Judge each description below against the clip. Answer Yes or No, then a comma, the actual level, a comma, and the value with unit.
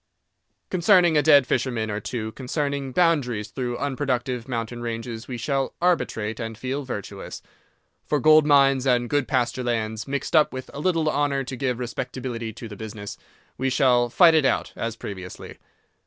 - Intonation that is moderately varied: Yes, average, 3.6 semitones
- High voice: No, low, 130 Hz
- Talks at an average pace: Yes, average, 165 wpm